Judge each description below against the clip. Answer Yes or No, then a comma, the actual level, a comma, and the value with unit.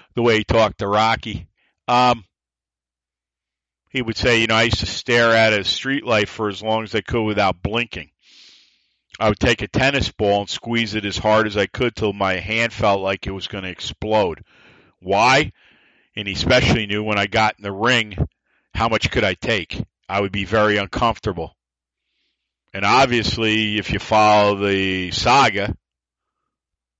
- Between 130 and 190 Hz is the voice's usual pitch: No, low, 105 Hz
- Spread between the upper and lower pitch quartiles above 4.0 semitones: No, average, 3.0 semitones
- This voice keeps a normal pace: Yes, average, 180 wpm